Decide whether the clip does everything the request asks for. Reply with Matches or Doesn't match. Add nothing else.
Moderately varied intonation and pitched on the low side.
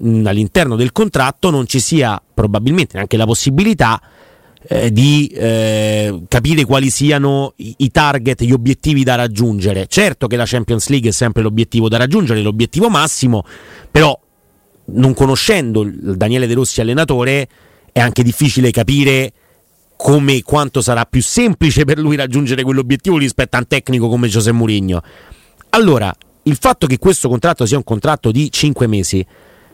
Matches